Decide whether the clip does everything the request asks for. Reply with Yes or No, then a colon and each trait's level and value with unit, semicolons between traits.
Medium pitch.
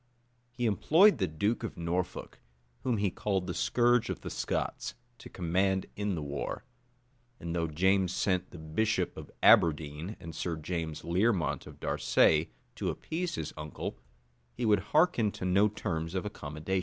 No: very low, 90 Hz